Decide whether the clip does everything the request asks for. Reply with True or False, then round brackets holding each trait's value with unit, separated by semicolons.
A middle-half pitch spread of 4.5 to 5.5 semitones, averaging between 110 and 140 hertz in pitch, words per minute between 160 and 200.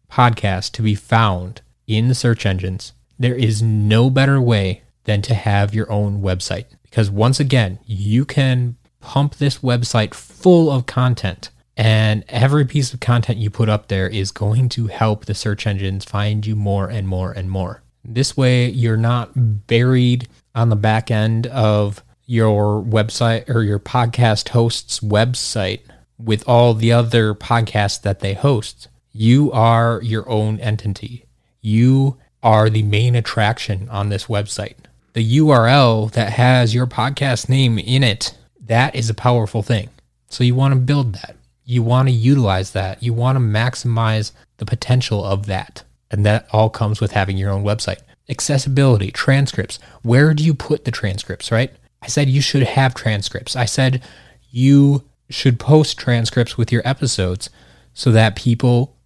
False (2.9 semitones; 115 Hz; 165 wpm)